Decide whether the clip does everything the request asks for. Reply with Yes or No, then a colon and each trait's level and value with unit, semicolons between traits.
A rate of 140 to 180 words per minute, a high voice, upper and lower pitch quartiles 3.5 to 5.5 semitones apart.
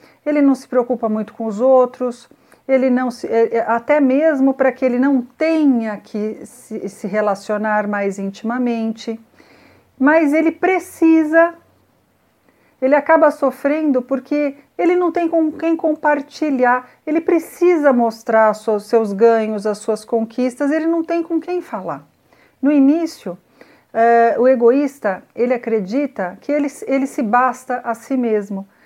No: average, 130 wpm; very high, 255 Hz; average, 4.8 semitones